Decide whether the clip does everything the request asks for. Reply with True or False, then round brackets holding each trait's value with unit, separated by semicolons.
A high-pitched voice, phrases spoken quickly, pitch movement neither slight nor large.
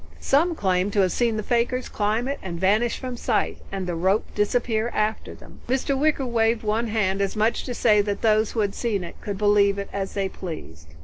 True (215 Hz; 225 wpm; 3.2 semitones)